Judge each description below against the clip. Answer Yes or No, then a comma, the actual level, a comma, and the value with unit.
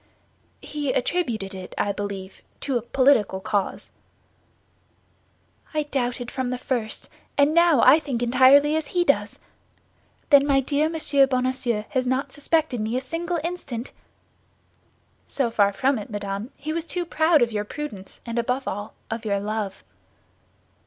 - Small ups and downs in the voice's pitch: No, average, 5.2 semitones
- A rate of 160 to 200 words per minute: No, average, 150 wpm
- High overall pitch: Yes, very high, 255 Hz